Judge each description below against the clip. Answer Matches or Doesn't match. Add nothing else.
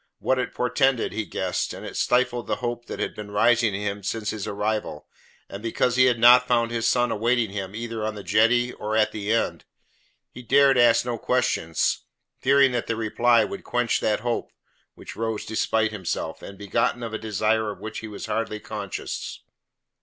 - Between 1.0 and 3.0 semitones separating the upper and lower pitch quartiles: Matches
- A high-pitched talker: Doesn't match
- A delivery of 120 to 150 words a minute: Doesn't match